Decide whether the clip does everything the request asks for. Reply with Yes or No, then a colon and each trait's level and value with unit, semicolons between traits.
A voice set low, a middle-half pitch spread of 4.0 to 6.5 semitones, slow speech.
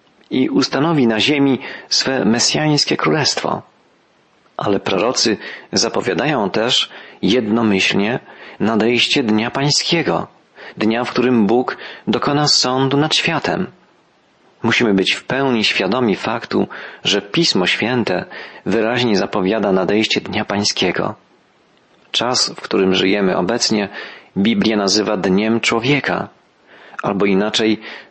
Yes: low, 115 Hz; average, 4.6 semitones; slow, 100 wpm